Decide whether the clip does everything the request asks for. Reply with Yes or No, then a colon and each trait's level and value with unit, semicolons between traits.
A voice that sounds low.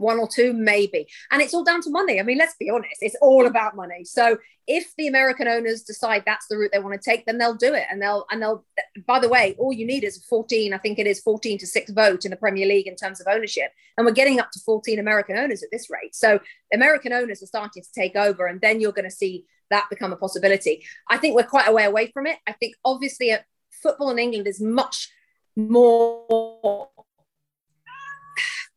No: high, 225 Hz